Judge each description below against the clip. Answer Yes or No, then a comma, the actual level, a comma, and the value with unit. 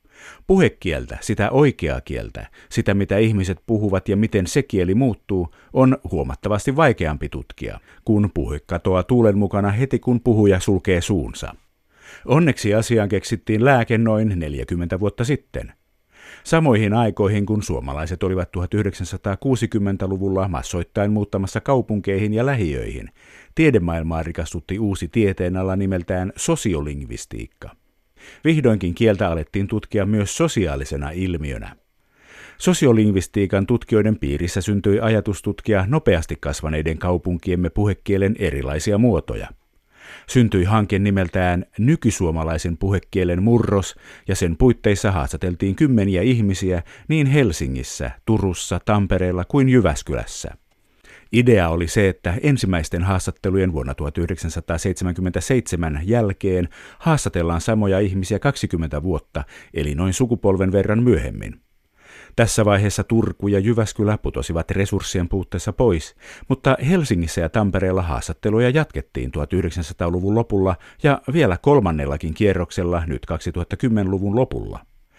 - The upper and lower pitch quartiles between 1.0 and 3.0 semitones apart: No, average, 4.0 semitones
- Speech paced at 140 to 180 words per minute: No, average, 105 wpm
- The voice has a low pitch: Yes, low, 100 Hz